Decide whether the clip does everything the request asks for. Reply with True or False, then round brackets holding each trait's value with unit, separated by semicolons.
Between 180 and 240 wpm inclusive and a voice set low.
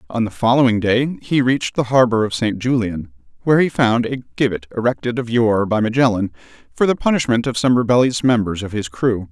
True (200 wpm; 120 Hz)